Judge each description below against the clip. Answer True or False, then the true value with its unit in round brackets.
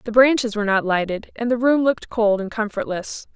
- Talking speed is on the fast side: True (215 wpm)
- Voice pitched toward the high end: True (225 Hz)